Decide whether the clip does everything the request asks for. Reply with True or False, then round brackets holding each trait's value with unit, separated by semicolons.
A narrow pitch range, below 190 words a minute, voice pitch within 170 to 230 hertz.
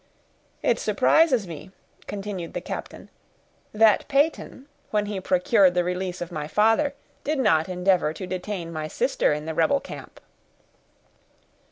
False (4.0 semitones; 140 wpm; 190 Hz)